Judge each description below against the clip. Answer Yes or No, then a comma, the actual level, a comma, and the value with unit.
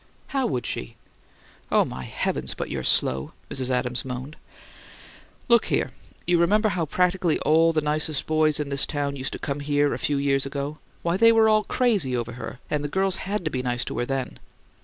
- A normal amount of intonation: Yes, average, 4.8 semitones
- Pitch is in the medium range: Yes, medium, 150 Hz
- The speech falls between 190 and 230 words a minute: Yes, average, 200 wpm